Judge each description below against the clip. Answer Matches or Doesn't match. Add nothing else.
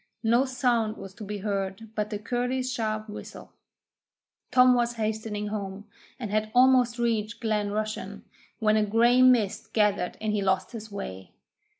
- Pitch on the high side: Matches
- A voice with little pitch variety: Matches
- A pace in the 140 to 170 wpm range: Matches